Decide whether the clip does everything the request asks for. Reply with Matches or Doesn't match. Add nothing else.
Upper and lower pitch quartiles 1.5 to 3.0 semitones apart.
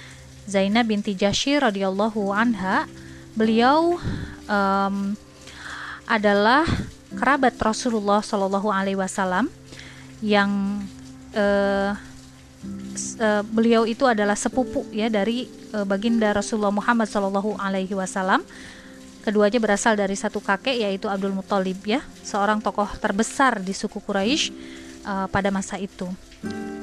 Matches